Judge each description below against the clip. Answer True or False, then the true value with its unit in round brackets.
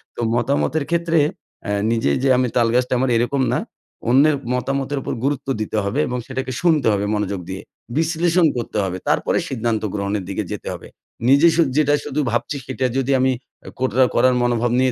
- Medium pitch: False (130 Hz)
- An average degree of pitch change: True (3.6 semitones)